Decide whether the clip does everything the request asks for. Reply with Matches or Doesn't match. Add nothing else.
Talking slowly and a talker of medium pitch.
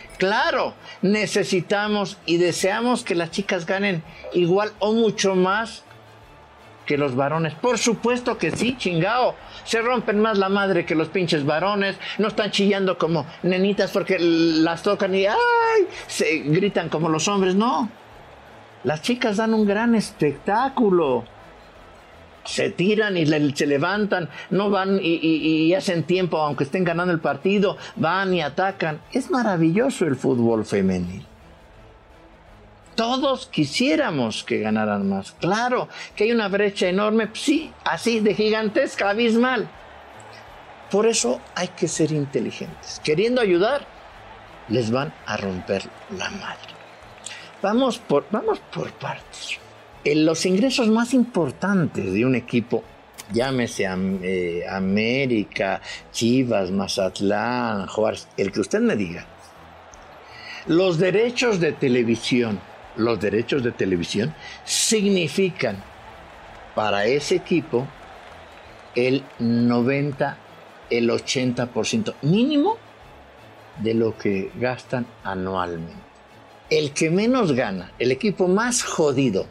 Matches